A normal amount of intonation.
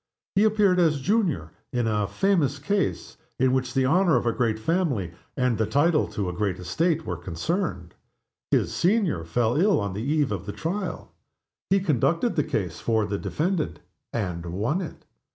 No: wide, 8.9 semitones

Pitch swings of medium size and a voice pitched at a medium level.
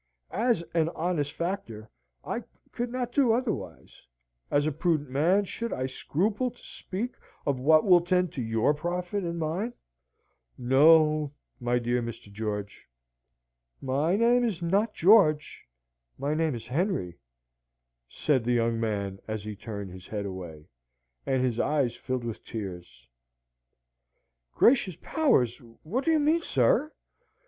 No: wide, 8.8 semitones; medium, 150 Hz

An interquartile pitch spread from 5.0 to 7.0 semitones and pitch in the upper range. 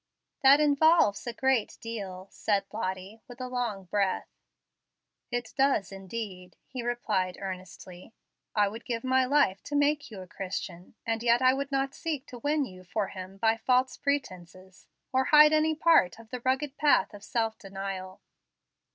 Yes: wide, 5.6 semitones; high, 230 Hz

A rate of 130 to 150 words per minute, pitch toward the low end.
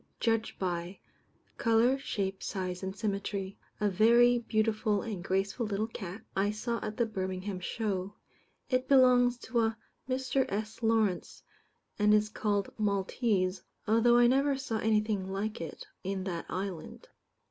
No: average, 140 wpm; high, 215 Hz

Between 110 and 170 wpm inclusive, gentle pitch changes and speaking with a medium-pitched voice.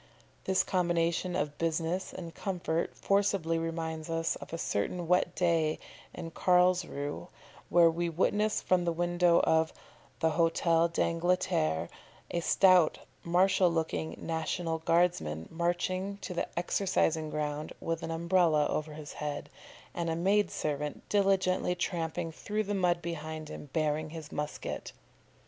Yes: slow, 135 wpm; narrow, 2.1 semitones; medium, 165 Hz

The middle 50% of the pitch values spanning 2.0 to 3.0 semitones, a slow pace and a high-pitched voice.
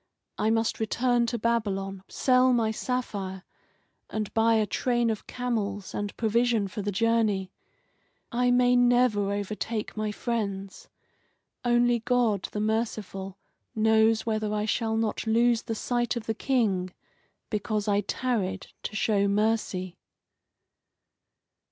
Yes: narrow, 2.6 semitones; slow, 125 wpm; high, 220 Hz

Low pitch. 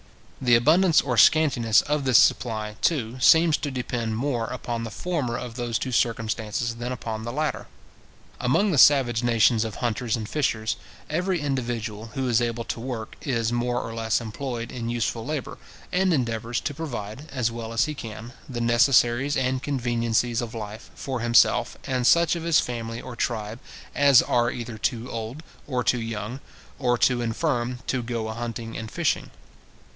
Yes: low, 120 Hz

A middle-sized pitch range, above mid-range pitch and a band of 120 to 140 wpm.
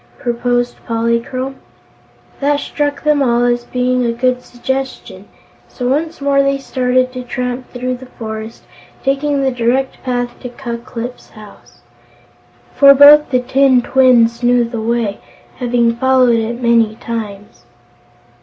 No: narrow, 2.1 semitones; very high, 250 Hz; slow, 135 wpm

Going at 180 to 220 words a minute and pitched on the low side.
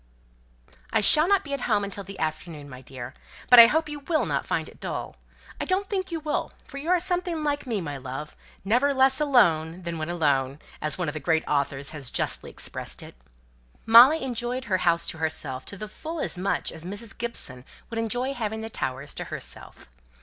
No: average, 200 wpm; high, 210 Hz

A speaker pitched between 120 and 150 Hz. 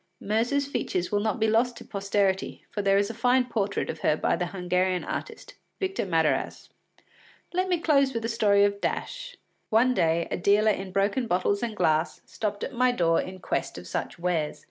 No: high, 205 Hz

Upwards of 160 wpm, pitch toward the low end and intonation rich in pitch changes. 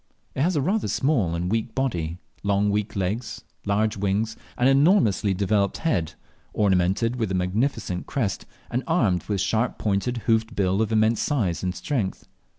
No: average, 170 wpm; low, 105 Hz; average, 4.3 semitones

